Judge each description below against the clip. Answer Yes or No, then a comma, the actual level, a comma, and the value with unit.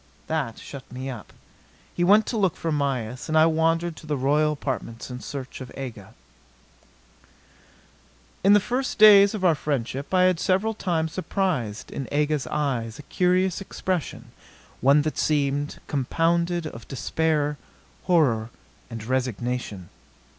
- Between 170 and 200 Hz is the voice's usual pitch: No, medium, 150 Hz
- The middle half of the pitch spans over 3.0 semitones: Yes, average, 5.3 semitones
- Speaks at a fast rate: No, average, 140 wpm